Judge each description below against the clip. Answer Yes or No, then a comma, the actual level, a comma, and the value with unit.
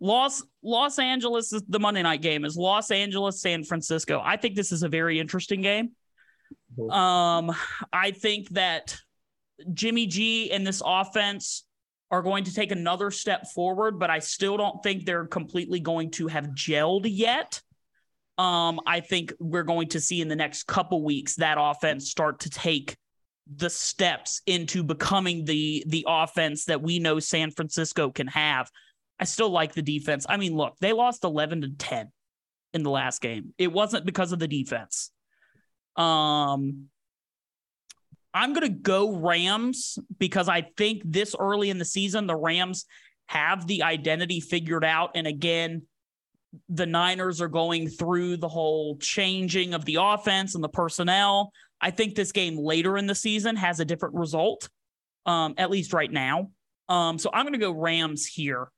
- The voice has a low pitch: No, medium, 175 Hz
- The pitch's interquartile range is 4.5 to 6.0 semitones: No, average, 3.6 semitones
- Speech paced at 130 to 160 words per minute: No, average, 170 wpm